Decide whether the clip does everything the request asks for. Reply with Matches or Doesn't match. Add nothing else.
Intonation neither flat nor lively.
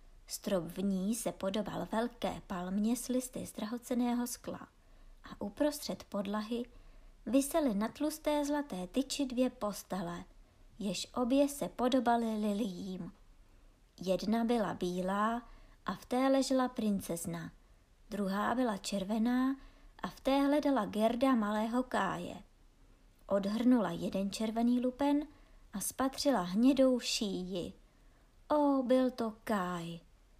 Matches